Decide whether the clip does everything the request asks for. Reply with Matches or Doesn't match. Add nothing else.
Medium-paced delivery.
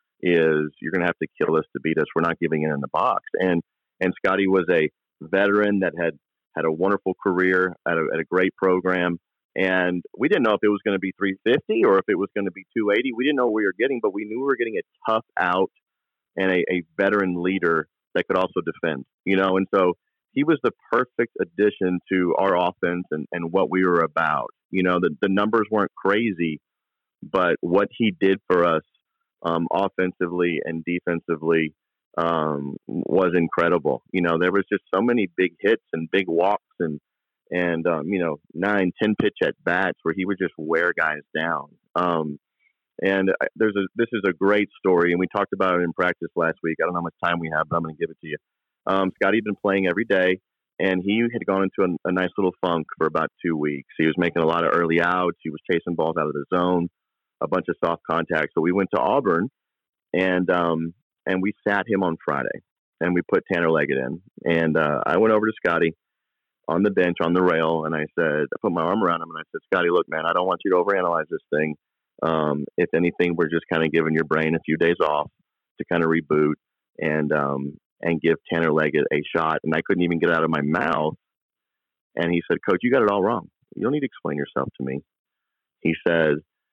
Doesn't match